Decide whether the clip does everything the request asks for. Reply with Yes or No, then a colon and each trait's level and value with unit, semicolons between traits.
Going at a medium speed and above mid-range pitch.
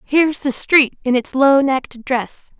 Yes: average, 185 wpm; very high, 270 Hz